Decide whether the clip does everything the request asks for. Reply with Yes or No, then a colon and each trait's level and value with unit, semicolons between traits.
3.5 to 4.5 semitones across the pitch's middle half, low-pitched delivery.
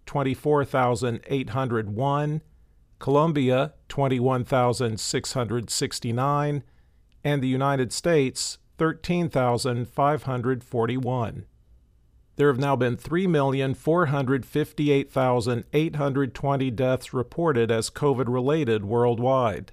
No: average, 2.8 semitones; low, 130 Hz